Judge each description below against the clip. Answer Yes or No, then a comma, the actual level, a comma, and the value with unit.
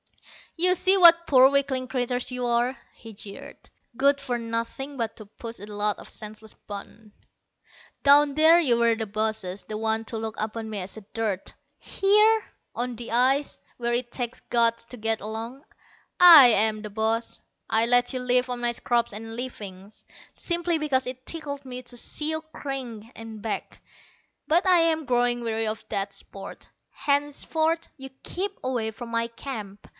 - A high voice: Yes, high, 240 Hz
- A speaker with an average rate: Yes, average, 170 wpm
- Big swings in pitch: No, average, 4.0 semitones